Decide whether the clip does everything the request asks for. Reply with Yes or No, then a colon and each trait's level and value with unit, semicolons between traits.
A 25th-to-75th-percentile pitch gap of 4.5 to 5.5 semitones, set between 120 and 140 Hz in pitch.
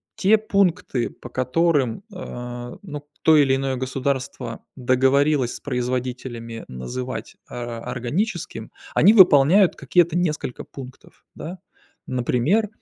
Yes: average, 5.2 semitones; low, 135 Hz